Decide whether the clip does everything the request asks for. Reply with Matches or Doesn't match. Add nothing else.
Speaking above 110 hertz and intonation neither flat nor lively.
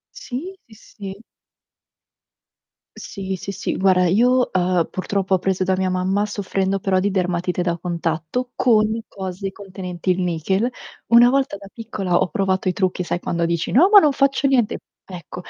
Matches